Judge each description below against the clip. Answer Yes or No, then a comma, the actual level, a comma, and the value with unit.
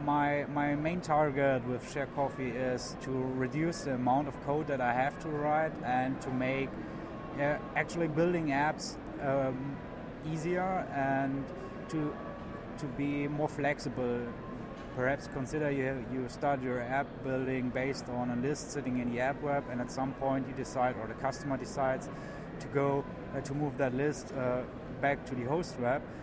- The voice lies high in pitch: No, low, 135 Hz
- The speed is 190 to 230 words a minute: No, average, 170 wpm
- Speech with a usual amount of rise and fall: No, narrow, 2.1 semitones